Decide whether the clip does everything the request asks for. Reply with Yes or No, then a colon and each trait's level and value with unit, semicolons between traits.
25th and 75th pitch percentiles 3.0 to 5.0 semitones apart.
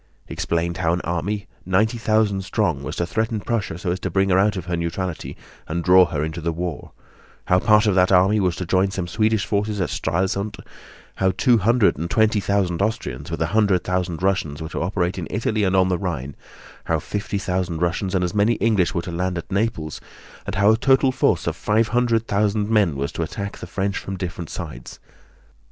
Yes: average, 3.3 semitones